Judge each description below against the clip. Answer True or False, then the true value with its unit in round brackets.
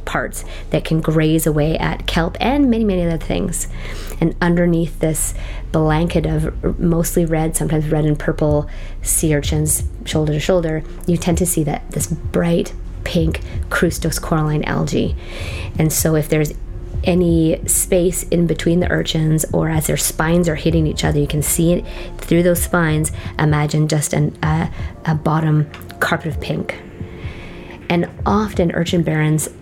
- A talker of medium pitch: True (155 Hz)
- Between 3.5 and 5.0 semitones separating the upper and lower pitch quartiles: False (2.8 semitones)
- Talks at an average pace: True (155 wpm)